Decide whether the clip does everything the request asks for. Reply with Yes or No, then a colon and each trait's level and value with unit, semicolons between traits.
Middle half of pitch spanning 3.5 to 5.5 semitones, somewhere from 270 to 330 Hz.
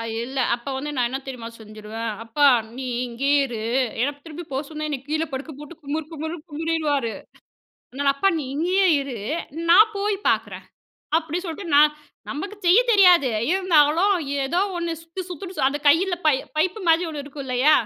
Yes: average, 4.1 semitones; very high, 300 Hz